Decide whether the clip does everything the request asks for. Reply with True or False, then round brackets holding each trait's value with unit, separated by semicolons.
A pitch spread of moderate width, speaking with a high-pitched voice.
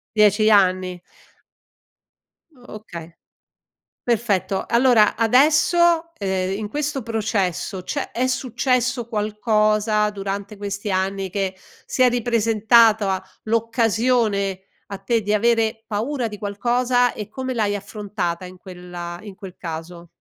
True (3.4 semitones; 210 Hz)